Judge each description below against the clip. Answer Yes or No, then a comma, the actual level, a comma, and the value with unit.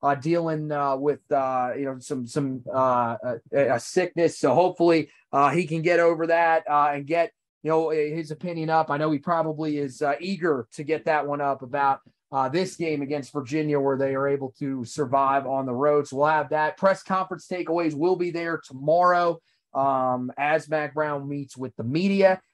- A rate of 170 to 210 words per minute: Yes, average, 200 wpm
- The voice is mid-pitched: Yes, medium, 150 Hz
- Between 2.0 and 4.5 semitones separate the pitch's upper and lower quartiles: Yes, average, 3.2 semitones